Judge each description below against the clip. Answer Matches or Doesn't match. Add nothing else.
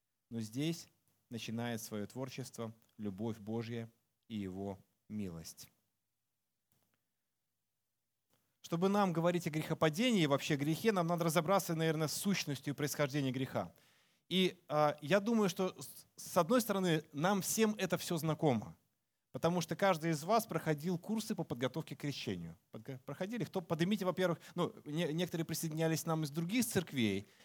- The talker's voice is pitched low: Doesn't match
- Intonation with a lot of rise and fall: Matches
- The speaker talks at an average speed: Matches